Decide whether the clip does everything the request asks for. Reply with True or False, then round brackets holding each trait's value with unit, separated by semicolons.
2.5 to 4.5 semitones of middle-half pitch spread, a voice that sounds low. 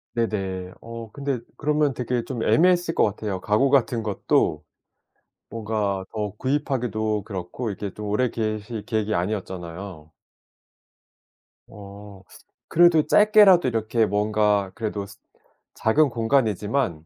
True (4.0 semitones; 110 Hz)